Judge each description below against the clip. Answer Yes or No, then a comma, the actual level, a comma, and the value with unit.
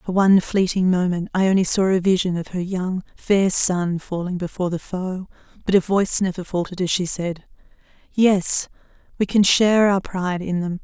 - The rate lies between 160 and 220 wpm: Yes, average, 185 wpm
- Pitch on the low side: No, medium, 185 Hz